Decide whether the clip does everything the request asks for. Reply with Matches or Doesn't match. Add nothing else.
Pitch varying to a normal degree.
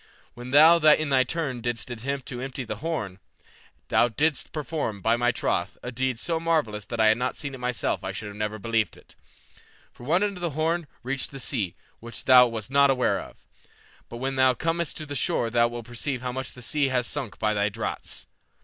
Matches